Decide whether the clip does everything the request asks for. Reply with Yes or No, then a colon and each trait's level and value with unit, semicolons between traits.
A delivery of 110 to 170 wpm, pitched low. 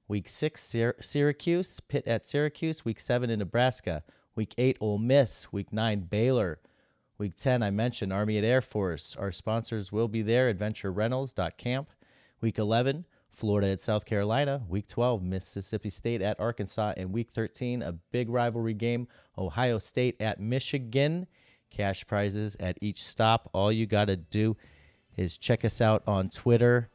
Yes: average, 160 wpm; low, 110 Hz